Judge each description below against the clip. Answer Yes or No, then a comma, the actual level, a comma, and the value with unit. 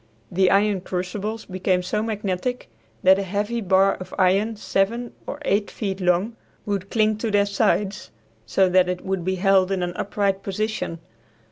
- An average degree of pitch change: No, narrow, 2.2 semitones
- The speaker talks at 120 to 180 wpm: Yes, average, 165 wpm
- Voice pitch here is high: Yes, high, 195 Hz